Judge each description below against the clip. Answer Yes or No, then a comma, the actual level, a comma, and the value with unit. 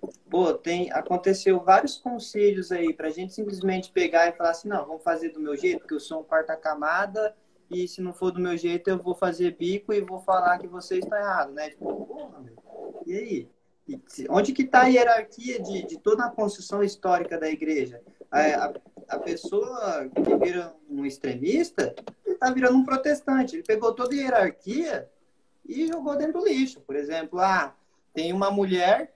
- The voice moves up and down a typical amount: No, wide, 6.7 semitones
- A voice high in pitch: Yes, high, 195 Hz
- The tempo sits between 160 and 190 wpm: Yes, average, 180 wpm